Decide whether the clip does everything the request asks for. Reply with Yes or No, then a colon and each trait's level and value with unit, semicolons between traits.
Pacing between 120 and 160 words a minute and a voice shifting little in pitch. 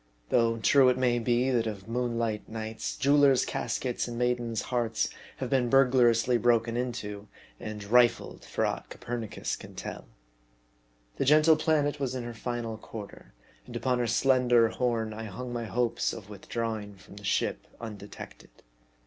Yes: average, 155 wpm; narrow, 2.1 semitones